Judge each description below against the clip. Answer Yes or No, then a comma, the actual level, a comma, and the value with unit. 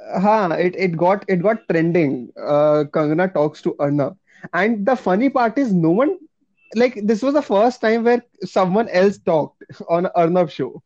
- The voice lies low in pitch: No, medium, 185 Hz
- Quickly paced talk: No, average, 175 wpm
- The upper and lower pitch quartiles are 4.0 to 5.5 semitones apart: Yes, average, 5.1 semitones